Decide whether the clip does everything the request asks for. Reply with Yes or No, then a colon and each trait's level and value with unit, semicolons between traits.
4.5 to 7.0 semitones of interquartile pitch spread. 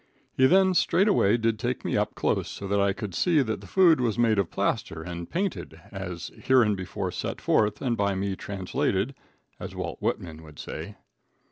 Yes: average, 5.3 semitones